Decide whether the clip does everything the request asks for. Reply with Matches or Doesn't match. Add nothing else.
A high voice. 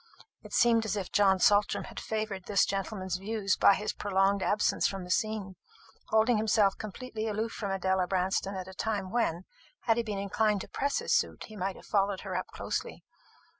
Matches